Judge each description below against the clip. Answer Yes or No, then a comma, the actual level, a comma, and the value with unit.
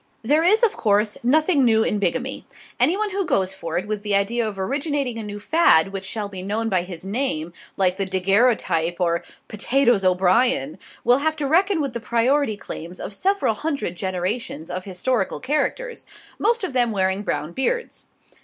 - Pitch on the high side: Yes, high, 220 Hz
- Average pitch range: No, wide, 6.7 semitones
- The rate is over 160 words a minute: Yes, average, 180 wpm